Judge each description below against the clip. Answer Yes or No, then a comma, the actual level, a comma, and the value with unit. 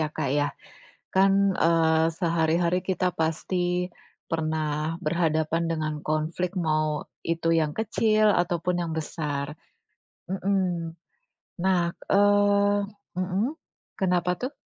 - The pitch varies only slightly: No, average, 3.0 semitones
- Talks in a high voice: No, medium, 170 Hz